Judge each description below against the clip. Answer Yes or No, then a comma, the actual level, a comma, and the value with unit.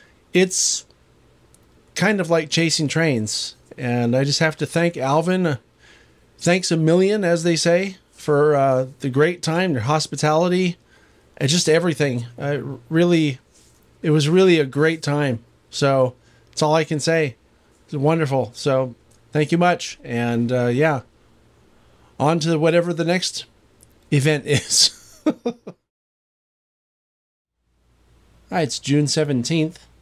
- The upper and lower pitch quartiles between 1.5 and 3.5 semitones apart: No, average, 4.4 semitones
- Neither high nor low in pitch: Yes, medium, 155 Hz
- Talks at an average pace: No, slow, 125 wpm